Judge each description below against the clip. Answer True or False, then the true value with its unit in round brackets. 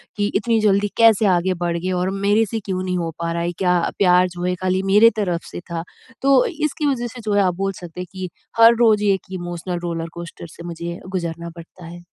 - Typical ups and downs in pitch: True (3.3 semitones)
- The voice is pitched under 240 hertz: True (185 Hz)